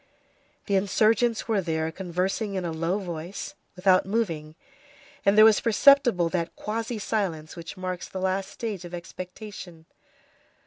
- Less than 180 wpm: Yes, average, 140 wpm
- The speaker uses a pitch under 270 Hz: Yes, high, 190 Hz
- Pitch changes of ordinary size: Yes, average, 3.8 semitones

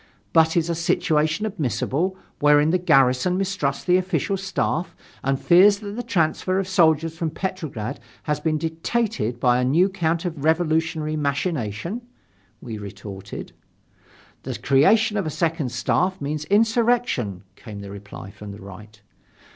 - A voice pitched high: No, medium, 160 Hz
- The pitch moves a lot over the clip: Yes, wide, 5.7 semitones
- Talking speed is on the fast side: No, average, 140 wpm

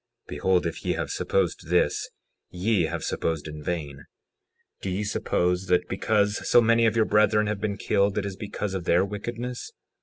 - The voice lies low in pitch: Yes, low, 100 Hz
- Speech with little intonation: No, average, 3.2 semitones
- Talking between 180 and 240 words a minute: Yes, average, 185 wpm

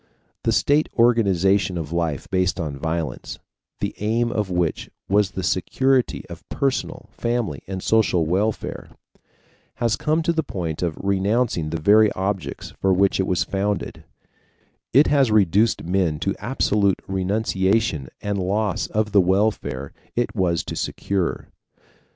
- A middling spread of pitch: Yes, average, 3.6 semitones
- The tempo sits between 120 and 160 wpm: Yes, average, 140 wpm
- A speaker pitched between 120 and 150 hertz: No, low, 100 Hz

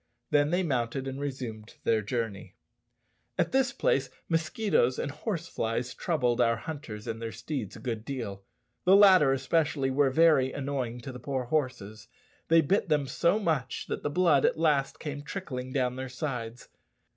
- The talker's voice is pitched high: No, low, 135 Hz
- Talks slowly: No, average, 170 wpm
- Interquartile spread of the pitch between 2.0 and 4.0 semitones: No, average, 4.6 semitones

